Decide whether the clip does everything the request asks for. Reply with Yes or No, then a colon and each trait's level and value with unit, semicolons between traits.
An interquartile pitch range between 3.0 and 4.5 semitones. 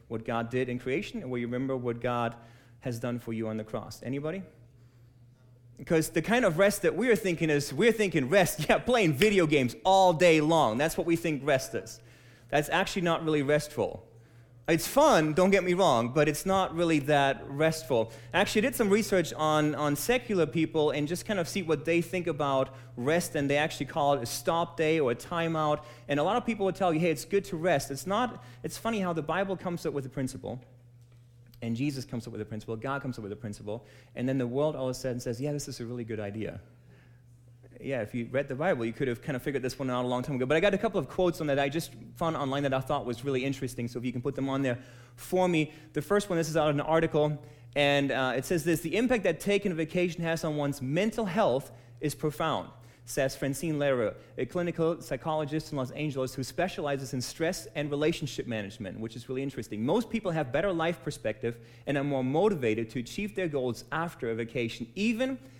No: average, 5.3 semitones